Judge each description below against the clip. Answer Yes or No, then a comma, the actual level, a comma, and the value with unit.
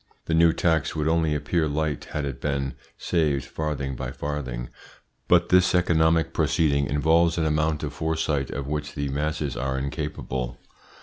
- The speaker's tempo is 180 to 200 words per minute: No, average, 160 wpm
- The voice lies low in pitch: Yes, very low, 75 Hz